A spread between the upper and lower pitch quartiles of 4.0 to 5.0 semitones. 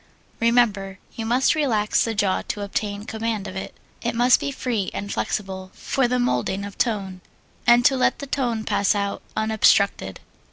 No: average, 3.2 semitones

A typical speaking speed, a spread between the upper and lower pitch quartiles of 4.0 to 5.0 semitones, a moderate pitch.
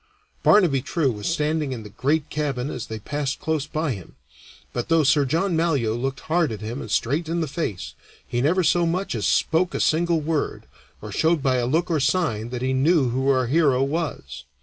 No: fast, 215 wpm; average, 4.6 semitones; medium, 145 Hz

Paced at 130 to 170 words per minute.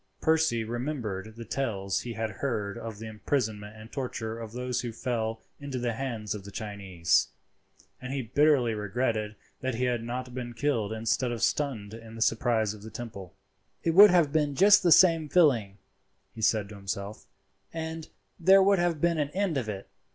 No: average, 185 wpm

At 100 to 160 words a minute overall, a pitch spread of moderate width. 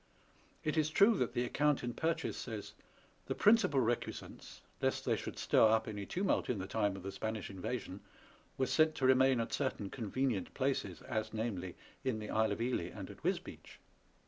No: average, 190 wpm; average, 4.2 semitones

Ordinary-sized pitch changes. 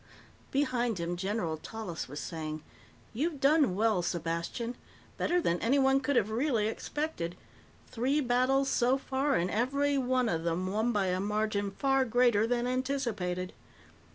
No: wide, 6.4 semitones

